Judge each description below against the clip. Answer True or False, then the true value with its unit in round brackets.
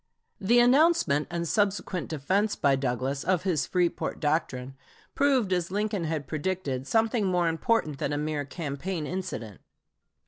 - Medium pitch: True (170 Hz)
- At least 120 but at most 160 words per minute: True (140 wpm)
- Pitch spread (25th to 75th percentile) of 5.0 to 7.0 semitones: True (5.6 semitones)